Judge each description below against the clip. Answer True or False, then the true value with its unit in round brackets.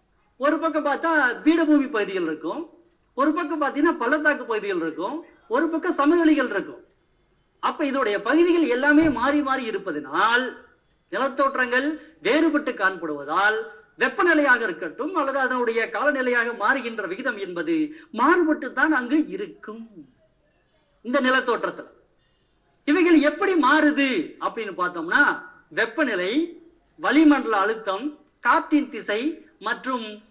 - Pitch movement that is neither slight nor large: False (5.7 semitones)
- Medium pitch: False (285 Hz)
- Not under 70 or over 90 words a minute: False (100 wpm)